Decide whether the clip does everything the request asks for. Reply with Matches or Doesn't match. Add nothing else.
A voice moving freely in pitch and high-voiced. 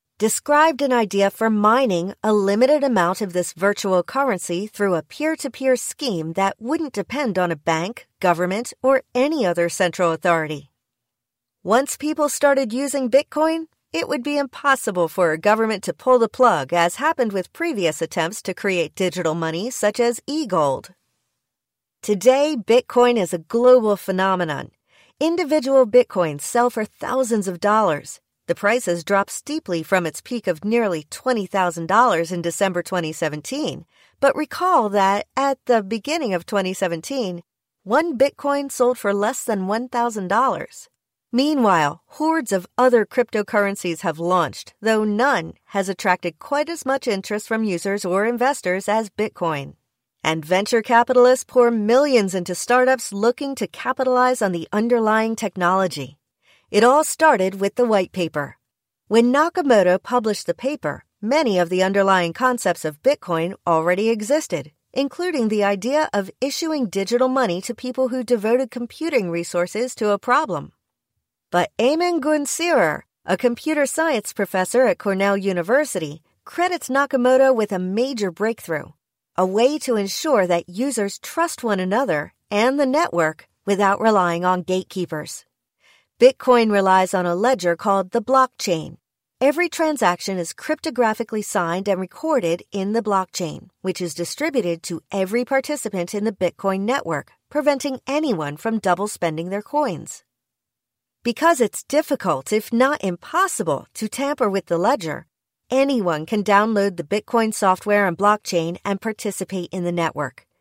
Matches